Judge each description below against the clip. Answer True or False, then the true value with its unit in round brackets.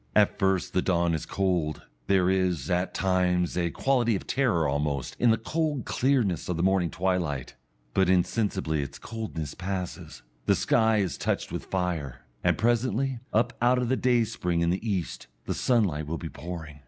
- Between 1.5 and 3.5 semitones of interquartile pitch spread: False (5.0 semitones)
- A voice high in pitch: False (95 Hz)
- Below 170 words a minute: False (175 wpm)